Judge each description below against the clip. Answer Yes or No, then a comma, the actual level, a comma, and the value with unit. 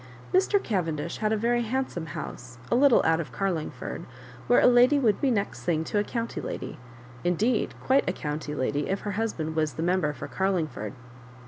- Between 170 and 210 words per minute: Yes, average, 200 wpm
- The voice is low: No, high, 190 Hz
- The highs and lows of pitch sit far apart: Yes, wide, 7.0 semitones